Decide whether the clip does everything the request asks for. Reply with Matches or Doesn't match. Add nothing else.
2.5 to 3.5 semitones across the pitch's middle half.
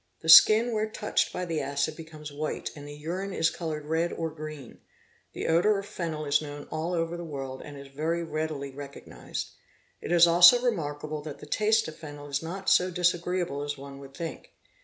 Matches